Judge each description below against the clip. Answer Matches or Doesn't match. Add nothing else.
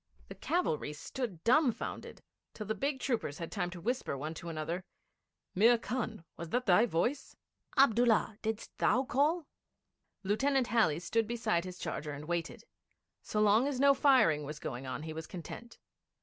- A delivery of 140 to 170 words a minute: Matches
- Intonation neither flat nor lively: Doesn't match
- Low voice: Doesn't match